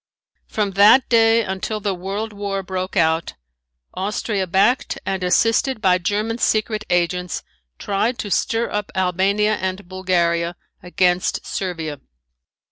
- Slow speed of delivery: Yes, slow, 125 wpm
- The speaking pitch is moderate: No, high, 195 Hz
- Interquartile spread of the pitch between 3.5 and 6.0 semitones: No, average, 2.8 semitones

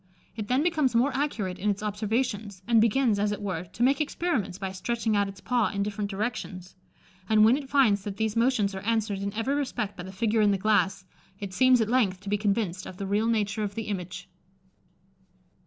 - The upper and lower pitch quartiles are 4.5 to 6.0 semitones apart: No, average, 2.9 semitones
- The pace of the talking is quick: Yes, fast, 215 wpm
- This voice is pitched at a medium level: No, high, 210 Hz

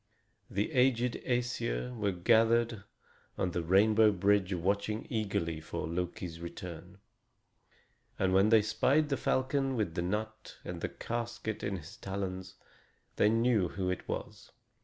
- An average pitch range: Yes, average, 4.1 semitones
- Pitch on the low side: Yes, low, 105 Hz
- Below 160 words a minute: Yes, average, 140 wpm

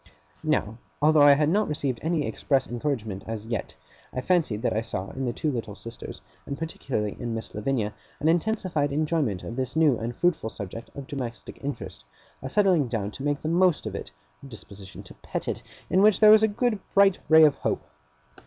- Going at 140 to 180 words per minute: No, average, 200 wpm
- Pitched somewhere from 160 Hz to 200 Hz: No, medium, 140 Hz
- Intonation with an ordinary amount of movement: No, wide, 6.0 semitones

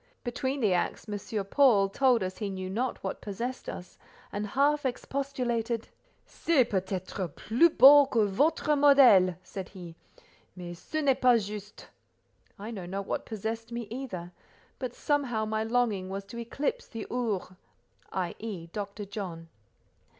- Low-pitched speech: No, high, 220 Hz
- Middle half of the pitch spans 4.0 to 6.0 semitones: Yes, average, 4.8 semitones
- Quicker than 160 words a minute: No, average, 150 wpm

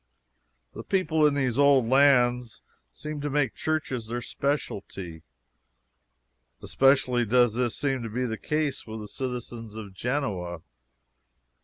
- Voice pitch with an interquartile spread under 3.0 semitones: No, average, 4.1 semitones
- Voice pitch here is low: Yes, low, 125 Hz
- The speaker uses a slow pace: Yes, slow, 130 wpm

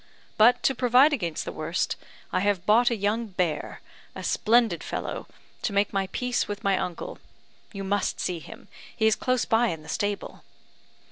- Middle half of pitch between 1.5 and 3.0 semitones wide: No, average, 3.8 semitones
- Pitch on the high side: Yes, high, 205 Hz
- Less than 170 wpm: No, average, 180 wpm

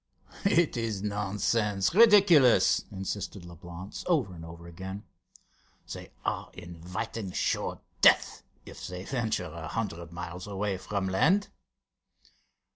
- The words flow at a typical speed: No, slow, 115 wpm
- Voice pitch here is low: Yes, very low, 95 Hz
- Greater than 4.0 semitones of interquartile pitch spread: Yes, average, 4.4 semitones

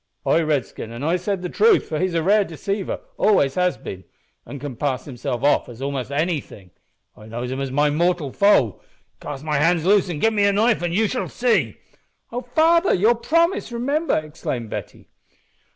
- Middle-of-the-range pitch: Yes, medium, 170 Hz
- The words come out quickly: No, average, 190 wpm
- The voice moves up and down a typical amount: No, wide, 7.2 semitones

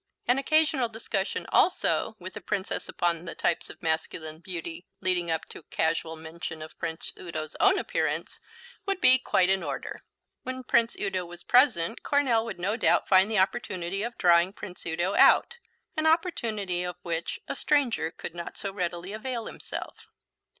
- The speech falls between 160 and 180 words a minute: Yes, average, 165 wpm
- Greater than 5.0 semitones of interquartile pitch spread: Yes, wide, 5.6 semitones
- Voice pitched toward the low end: No, high, 190 Hz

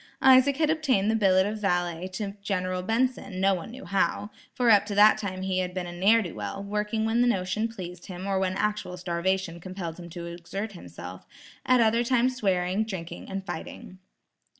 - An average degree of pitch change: Yes, average, 3.4 semitones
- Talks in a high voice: Yes, high, 195 Hz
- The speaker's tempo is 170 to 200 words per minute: Yes, average, 195 wpm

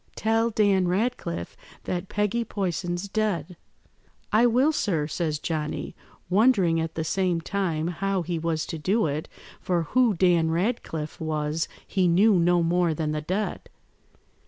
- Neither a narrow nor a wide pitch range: Yes, average, 4.0 semitones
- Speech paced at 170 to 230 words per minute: No, average, 145 wpm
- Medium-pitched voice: Yes, medium, 175 Hz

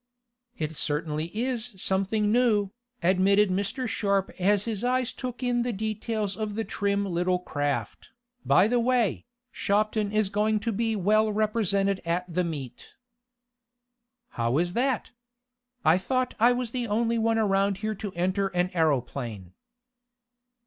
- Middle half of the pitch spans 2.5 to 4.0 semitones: Yes, average, 3.7 semitones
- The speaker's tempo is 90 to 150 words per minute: Yes, average, 140 wpm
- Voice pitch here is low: No, high, 205 Hz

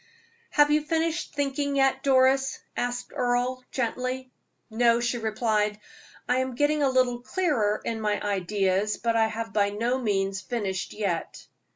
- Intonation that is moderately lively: Yes, average, 3.8 semitones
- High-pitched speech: Yes, high, 245 Hz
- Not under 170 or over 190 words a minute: No, average, 150 wpm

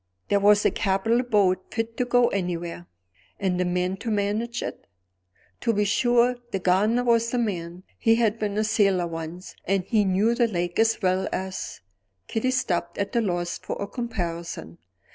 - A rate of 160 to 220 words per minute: Yes, average, 180 wpm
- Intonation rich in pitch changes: No, average, 4.2 semitones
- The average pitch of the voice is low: No, high, 200 Hz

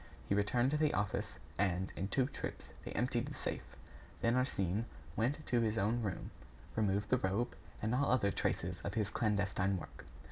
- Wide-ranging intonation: No, average, 3.7 semitones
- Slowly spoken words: No, average, 180 wpm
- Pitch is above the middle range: No, low, 105 Hz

